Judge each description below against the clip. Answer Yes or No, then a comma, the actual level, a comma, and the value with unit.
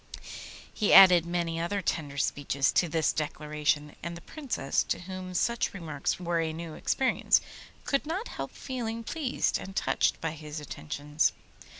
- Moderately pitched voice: Yes, medium, 170 Hz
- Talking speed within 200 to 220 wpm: No, average, 155 wpm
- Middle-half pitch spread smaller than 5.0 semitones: Yes, average, 4.5 semitones